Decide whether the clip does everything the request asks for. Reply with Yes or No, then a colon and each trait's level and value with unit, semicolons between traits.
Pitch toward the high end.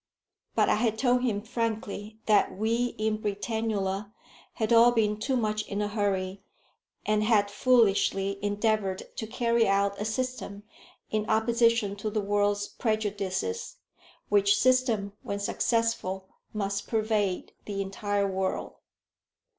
Yes: high, 210 Hz